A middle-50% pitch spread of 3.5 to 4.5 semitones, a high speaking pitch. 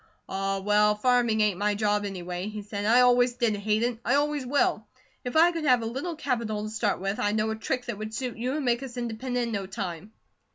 No: average, 3.1 semitones; high, 220 Hz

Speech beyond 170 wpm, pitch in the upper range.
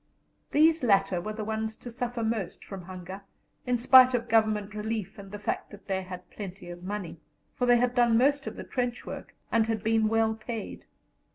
Yes: average, 200 wpm; high, 220 Hz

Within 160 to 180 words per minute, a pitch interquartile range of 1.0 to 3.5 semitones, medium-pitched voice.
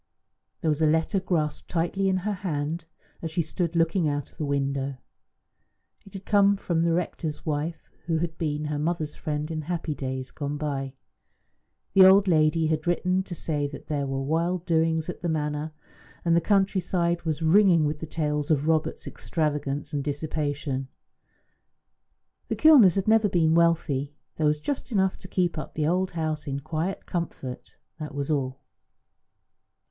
Yes: average, 175 wpm; average, 2.9 semitones; medium, 160 Hz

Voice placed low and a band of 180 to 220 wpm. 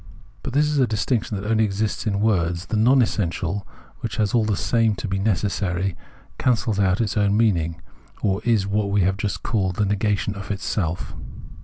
Yes: low, 105 Hz; average, 185 wpm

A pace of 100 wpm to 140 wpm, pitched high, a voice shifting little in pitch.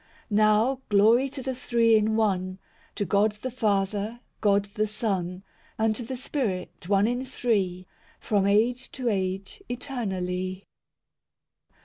No: slow, 135 wpm; high, 215 Hz; average, 3.5 semitones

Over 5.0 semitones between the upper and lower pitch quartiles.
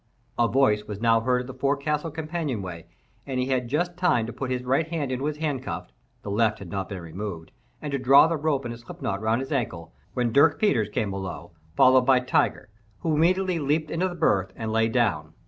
Yes: wide, 5.6 semitones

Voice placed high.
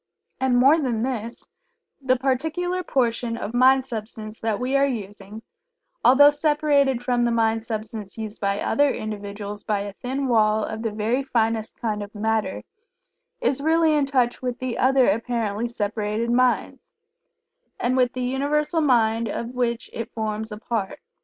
Yes: high, 235 Hz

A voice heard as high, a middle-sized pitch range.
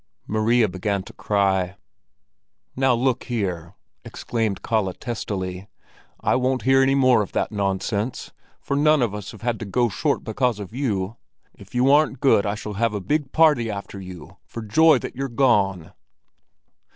No: low, 110 Hz; average, 4.5 semitones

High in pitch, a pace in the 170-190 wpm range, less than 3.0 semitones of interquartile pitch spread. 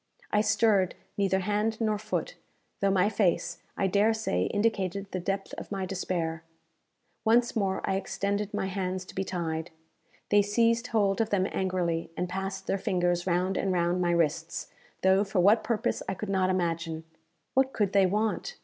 Yes: high, 195 Hz; average, 175 wpm; narrow, 2.6 semitones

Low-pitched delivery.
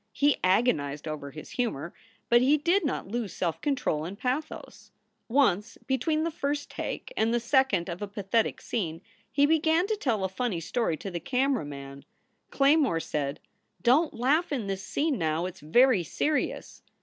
No: high, 235 Hz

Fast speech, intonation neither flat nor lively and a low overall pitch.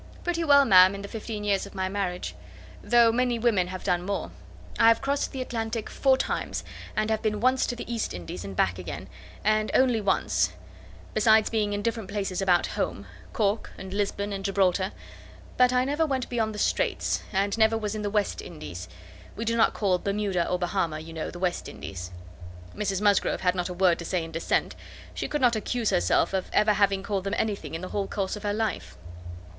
No: fast, 210 wpm; average, 3.4 semitones; high, 205 Hz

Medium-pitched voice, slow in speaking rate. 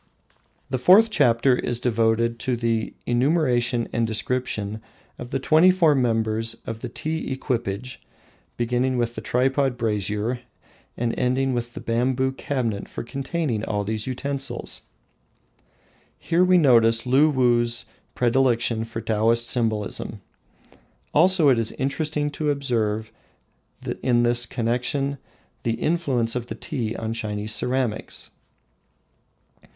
No: low, 120 Hz; slow, 120 wpm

